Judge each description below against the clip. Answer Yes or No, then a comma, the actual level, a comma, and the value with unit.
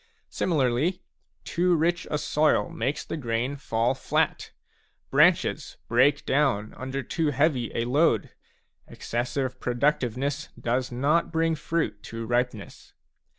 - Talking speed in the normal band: No, slow, 115 wpm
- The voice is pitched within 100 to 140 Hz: Yes, low, 135 Hz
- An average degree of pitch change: Yes, average, 4.0 semitones